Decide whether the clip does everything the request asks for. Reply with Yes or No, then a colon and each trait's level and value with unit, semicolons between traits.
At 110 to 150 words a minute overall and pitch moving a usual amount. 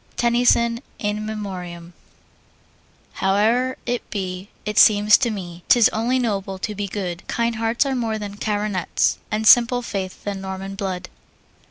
Yes: average, 145 wpm; average, 3.3 semitones